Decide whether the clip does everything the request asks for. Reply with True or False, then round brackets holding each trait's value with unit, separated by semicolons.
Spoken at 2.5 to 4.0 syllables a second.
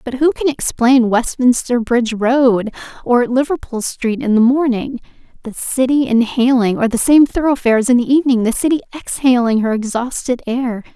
False (5.0 syllables/s)